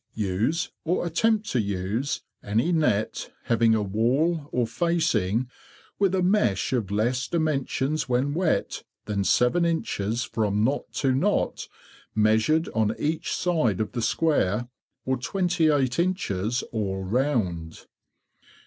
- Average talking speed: No, slow, 130 wpm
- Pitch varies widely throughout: Yes, wide, 7.0 semitones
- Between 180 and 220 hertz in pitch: No, low, 125 Hz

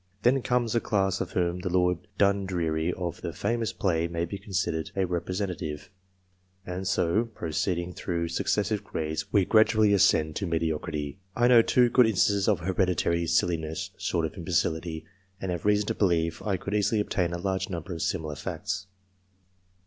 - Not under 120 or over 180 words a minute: Yes, average, 165 wpm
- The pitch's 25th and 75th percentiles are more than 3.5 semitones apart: No, average, 3.2 semitones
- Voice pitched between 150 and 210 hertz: No, very low, 90 Hz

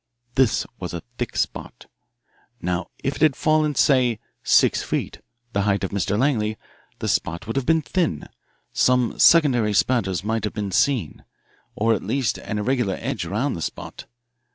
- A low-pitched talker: Yes, low, 115 Hz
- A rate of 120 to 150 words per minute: No, average, 165 wpm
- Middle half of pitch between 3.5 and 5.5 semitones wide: Yes, average, 5.1 semitones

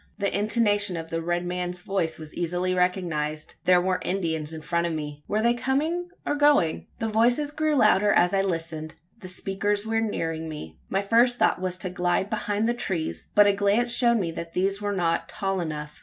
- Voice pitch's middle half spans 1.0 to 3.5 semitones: No, average, 4.3 semitones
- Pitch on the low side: No, high, 190 Hz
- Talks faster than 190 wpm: Yes, average, 200 wpm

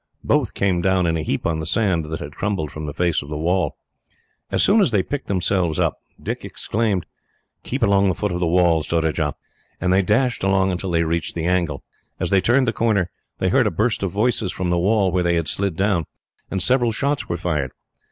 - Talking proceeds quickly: Yes, fast, 225 wpm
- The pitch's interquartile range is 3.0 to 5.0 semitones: Yes, average, 3.4 semitones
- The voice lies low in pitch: Yes, very low, 90 Hz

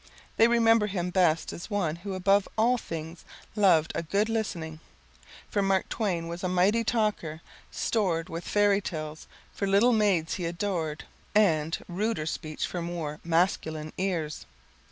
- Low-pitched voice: No, medium, 180 Hz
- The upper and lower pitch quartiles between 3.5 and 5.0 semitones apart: Yes, average, 4.0 semitones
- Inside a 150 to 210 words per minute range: Yes, average, 170 wpm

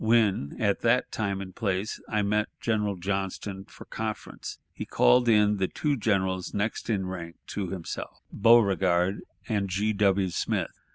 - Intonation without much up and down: Yes, narrow, 2.2 semitones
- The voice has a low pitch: Yes, low, 100 Hz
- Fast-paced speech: No, average, 155 wpm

